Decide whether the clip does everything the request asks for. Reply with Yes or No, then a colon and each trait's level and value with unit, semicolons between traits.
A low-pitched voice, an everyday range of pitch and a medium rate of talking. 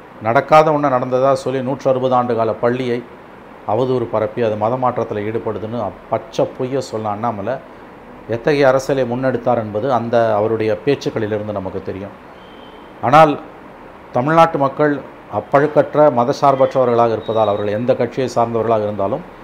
Yes: low, 125 Hz; average, 3.6 semitones; average, 115 wpm